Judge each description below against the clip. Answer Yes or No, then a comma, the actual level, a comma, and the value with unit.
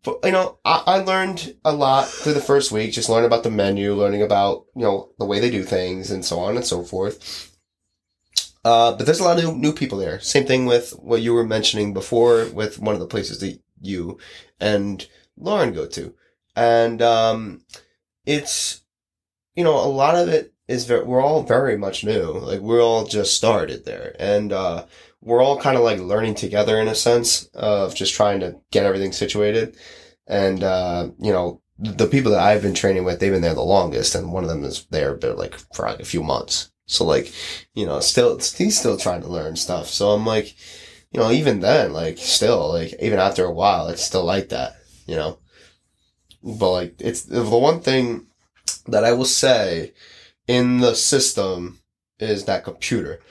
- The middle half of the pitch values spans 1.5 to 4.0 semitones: No, average, 5.2 semitones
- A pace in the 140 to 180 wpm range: No, average, 200 wpm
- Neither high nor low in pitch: No, low, 110 Hz